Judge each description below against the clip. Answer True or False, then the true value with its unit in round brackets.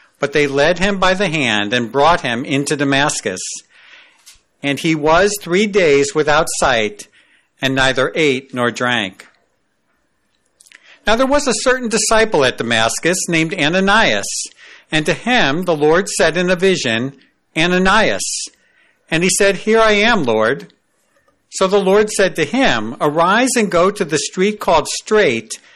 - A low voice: False (175 Hz)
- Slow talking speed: False (150 wpm)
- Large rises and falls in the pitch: True (6.8 semitones)